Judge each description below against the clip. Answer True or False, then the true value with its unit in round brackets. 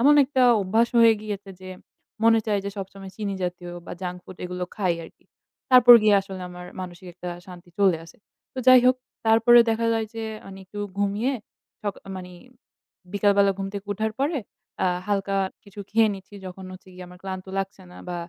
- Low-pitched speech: False (200 Hz)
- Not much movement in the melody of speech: False (3.1 semitones)